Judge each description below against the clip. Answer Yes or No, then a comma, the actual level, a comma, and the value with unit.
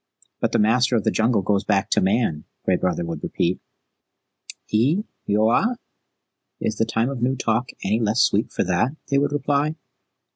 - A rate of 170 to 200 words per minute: Yes, average, 175 wpm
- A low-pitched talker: Yes, low, 115 Hz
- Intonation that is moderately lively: Yes, average, 4.6 semitones